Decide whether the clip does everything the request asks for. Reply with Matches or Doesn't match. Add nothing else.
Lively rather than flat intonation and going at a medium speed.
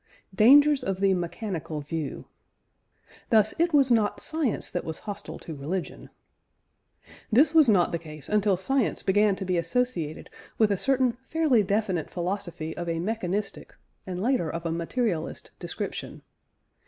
Matches